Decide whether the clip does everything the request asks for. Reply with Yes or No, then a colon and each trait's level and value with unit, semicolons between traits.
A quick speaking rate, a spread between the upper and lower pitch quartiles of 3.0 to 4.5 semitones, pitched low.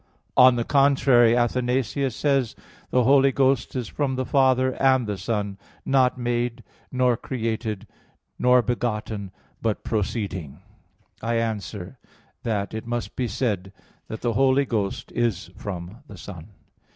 No: slow, 135 wpm; average, 3.4 semitones; low, 120 Hz